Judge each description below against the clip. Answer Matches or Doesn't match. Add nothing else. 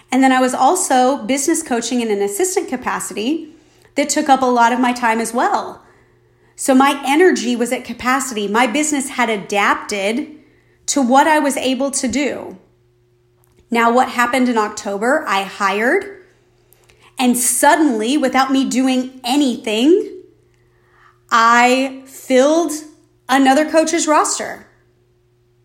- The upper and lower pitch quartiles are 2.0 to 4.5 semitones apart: Matches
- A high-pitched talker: Matches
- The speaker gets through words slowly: Matches